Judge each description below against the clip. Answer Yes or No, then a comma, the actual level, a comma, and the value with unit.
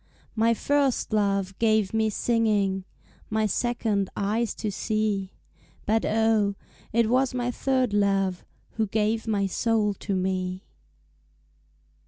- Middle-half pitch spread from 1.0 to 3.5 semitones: Yes, narrow, 2.4 semitones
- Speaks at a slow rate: Yes, slow, 120 wpm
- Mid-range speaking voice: No, high, 215 Hz